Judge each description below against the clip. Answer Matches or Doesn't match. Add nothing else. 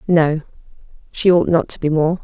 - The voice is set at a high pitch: Doesn't match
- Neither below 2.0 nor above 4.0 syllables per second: Doesn't match